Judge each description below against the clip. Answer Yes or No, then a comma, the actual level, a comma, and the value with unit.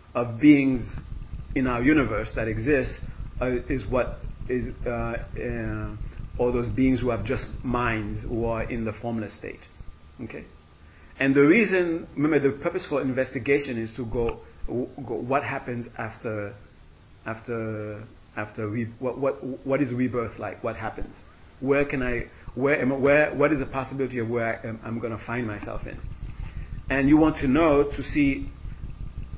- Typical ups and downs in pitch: Yes, average, 3.2 semitones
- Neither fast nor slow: Yes, average, 165 wpm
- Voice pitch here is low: Yes, low, 120 Hz